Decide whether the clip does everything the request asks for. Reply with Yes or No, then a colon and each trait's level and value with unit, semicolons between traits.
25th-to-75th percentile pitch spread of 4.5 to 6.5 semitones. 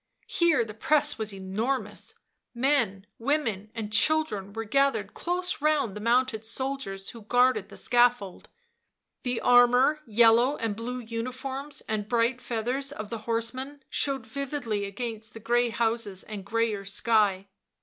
No: average, 3.6 semitones